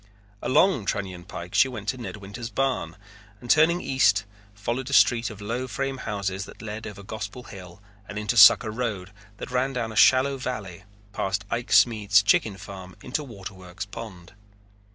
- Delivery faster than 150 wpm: Yes, average, 170 wpm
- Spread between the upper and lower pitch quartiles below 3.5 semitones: No, average, 4.2 semitones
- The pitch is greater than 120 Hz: No, low, 105 Hz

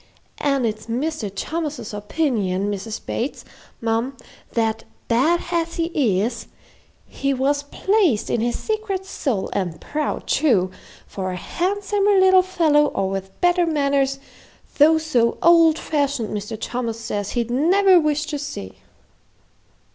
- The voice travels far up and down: Yes, wide, 6.7 semitones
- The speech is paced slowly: Yes, slow, 130 wpm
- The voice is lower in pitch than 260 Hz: No, very high, 275 Hz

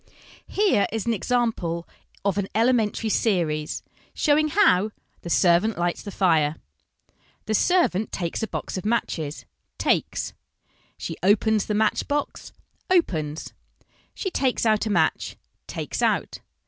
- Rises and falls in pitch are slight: No, average, 5.2 semitones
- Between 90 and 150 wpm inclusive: Yes, average, 145 wpm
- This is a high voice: Yes, high, 210 Hz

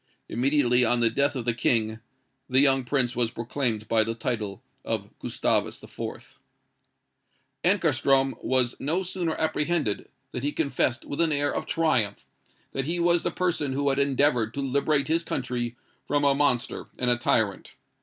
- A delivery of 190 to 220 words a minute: No, average, 165 wpm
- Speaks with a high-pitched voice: No, low, 135 Hz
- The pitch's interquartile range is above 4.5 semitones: No, average, 3.4 semitones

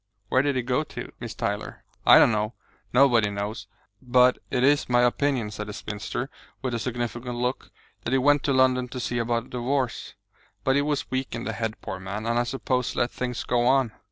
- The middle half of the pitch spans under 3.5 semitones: Yes, narrow, 2.4 semitones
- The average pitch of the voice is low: Yes, low, 125 Hz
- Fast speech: Yes, fast, 215 wpm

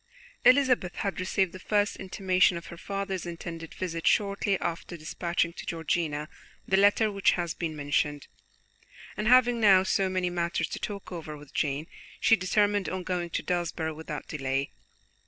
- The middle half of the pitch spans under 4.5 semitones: Yes, average, 3.2 semitones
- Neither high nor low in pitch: Yes, medium, 180 Hz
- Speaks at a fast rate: No, average, 160 wpm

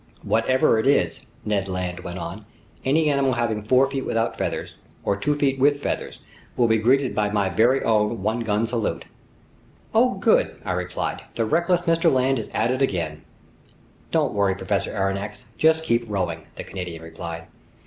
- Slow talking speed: No, average, 170 wpm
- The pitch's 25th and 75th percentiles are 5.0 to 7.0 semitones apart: Yes, average, 5.3 semitones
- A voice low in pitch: Yes, low, 110 Hz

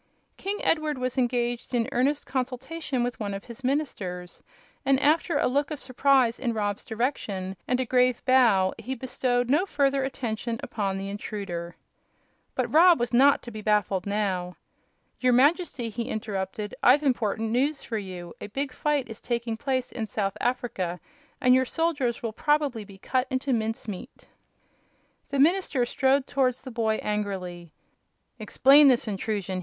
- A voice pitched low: No, high, 245 Hz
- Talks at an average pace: Yes, average, 160 wpm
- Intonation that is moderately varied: Yes, average, 4.3 semitones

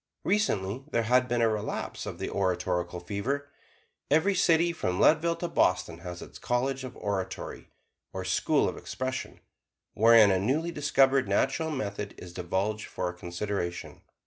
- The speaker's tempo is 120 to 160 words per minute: Yes, average, 150 wpm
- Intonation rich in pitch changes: Yes, wide, 6.6 semitones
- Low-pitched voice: Yes, low, 110 Hz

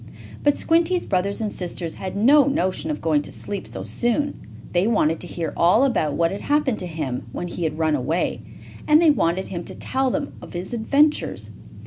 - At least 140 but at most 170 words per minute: No, average, 200 wpm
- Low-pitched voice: No, high, 190 Hz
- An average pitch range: No, wide, 8.5 semitones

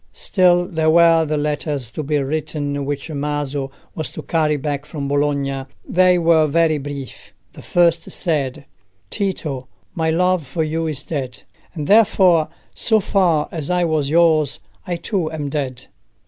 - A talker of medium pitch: Yes, medium, 155 Hz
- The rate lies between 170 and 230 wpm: No, average, 155 wpm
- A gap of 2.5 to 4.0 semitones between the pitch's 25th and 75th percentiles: Yes, average, 2.9 semitones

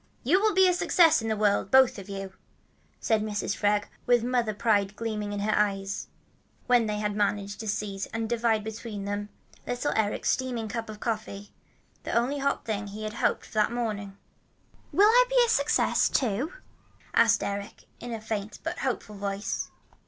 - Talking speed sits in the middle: Yes, average, 175 wpm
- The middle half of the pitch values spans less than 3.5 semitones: Yes, average, 2.9 semitones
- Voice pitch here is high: Yes, high, 215 Hz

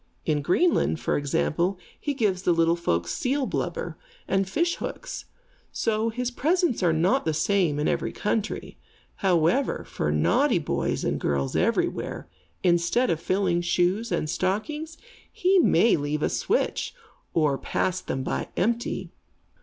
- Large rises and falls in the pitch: Yes, wide, 6.9 semitones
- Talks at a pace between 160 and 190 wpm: No, average, 145 wpm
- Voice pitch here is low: No, medium, 185 Hz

